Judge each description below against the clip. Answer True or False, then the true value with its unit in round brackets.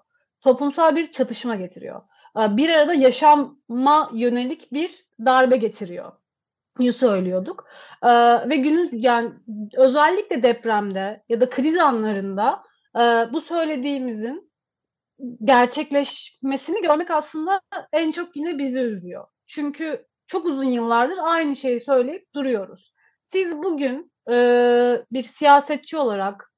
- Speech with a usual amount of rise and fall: True (4.6 semitones)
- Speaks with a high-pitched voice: True (265 Hz)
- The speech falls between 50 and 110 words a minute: True (100 wpm)